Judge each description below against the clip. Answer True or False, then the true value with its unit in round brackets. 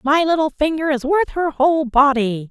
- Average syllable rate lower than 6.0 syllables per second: True (5.0 syllables/s)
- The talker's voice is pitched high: True (290 Hz)